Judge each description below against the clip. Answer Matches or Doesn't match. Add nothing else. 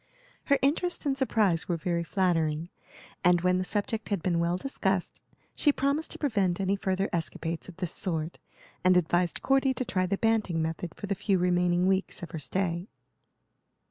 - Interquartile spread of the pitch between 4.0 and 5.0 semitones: Doesn't match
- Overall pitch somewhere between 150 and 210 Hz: Matches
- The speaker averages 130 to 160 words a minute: Doesn't match